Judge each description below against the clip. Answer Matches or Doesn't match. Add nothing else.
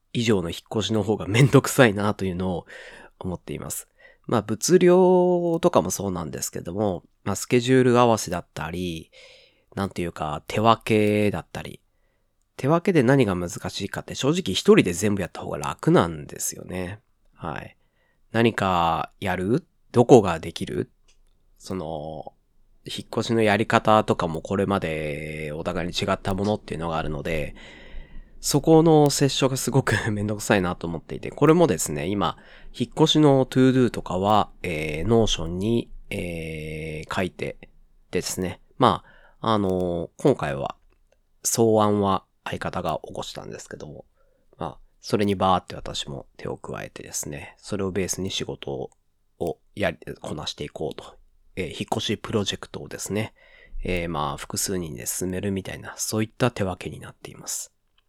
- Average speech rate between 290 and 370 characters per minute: Matches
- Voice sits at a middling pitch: Doesn't match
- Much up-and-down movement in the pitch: Doesn't match